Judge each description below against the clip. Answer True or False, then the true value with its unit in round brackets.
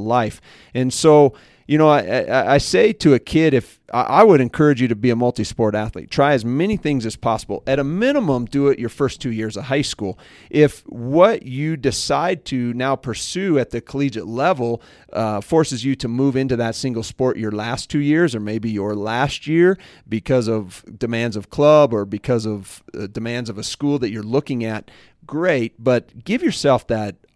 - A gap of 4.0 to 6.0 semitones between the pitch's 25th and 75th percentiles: True (4.4 semitones)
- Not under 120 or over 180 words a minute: False (195 wpm)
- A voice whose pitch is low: True (125 Hz)